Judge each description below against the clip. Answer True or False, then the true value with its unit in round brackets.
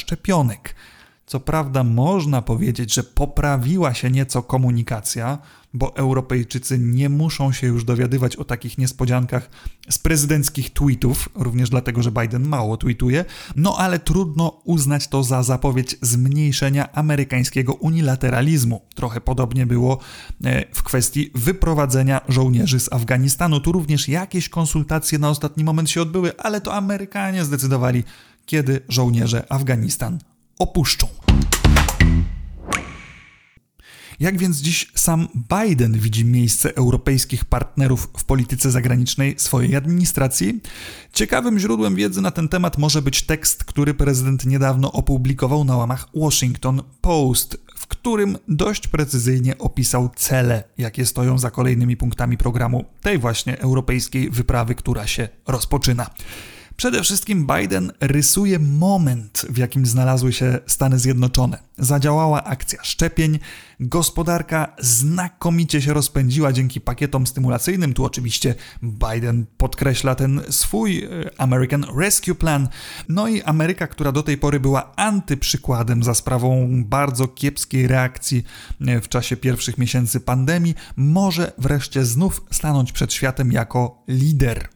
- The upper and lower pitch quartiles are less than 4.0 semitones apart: True (3.5 semitones)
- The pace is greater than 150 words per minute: False (120 wpm)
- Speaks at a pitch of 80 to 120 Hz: False (130 Hz)